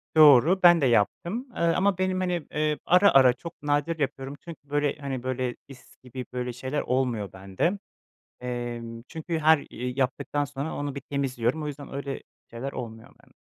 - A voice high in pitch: No, medium, 140 Hz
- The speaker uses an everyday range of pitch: Yes, average, 4.1 semitones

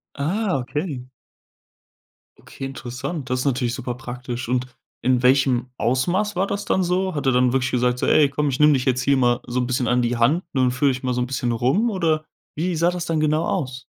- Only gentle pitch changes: No, average, 3.9 semitones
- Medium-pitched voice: No, low, 130 Hz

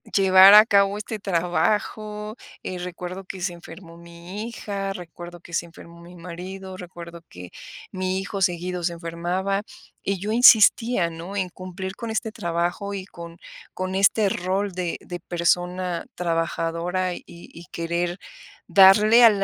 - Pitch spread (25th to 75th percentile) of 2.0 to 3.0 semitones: Yes, narrow, 2.4 semitones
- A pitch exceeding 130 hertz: Yes, medium, 185 Hz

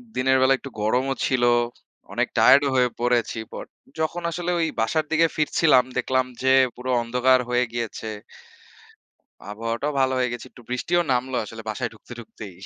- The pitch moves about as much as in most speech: No, narrow, 2.2 semitones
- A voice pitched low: Yes, low, 125 Hz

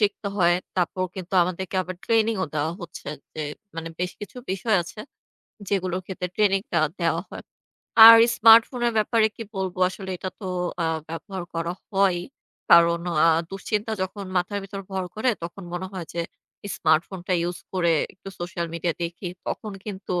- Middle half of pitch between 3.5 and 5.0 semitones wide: No, average, 2.8 semitones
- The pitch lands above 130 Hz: Yes, medium, 185 Hz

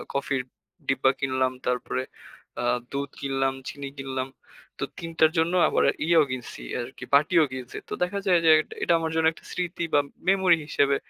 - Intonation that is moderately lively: Yes, average, 3.8 semitones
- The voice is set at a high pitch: No, medium, 140 Hz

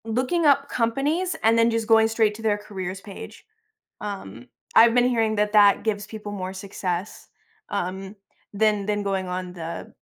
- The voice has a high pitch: Yes, high, 210 Hz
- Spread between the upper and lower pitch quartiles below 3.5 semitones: Yes, average, 2.9 semitones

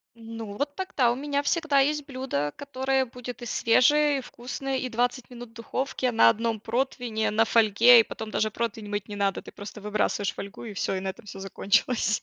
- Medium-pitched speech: No, high, 235 Hz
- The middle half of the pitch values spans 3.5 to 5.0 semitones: Yes, average, 3.8 semitones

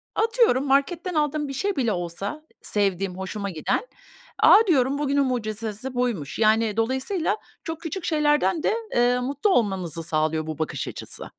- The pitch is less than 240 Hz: No, very high, 250 Hz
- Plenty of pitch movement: Yes, wide, 7.0 semitones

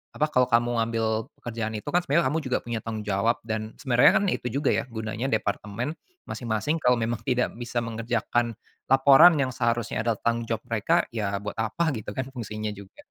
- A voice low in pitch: Yes, low, 115 Hz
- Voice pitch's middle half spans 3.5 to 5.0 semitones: No, narrow, 2.6 semitones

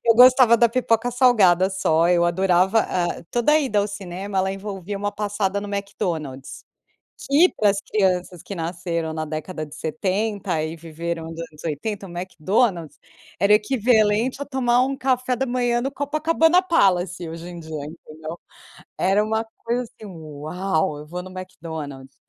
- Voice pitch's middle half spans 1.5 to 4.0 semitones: No, wide, 5.4 semitones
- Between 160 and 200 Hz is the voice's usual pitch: Yes, high, 195 Hz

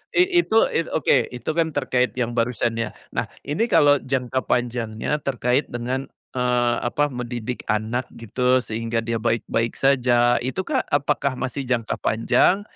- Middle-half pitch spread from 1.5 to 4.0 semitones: Yes, average, 2.9 semitones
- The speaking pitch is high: No, low, 125 Hz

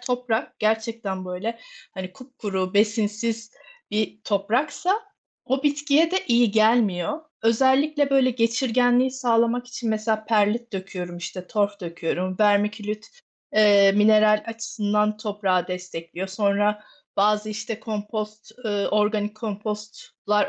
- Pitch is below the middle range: No, high, 215 Hz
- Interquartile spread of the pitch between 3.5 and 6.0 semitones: No, narrow, 2.4 semitones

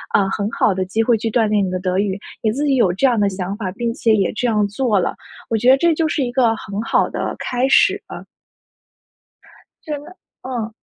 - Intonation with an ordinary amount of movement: Yes, average, 3.9 semitones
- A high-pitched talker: Yes, high, 225 Hz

